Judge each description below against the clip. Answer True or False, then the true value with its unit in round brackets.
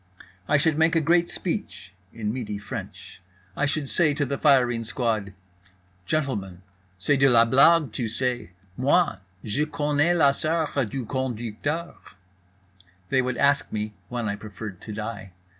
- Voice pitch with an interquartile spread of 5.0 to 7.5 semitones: True (5.3 semitones)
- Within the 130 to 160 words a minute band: True (150 wpm)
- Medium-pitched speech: False (130 Hz)